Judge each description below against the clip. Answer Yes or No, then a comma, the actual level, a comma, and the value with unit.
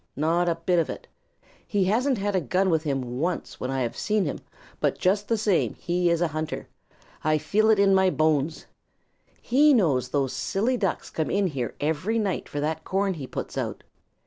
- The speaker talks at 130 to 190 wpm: No, average, 200 wpm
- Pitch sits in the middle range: Yes, medium, 175 Hz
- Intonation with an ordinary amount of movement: Yes, average, 4.7 semitones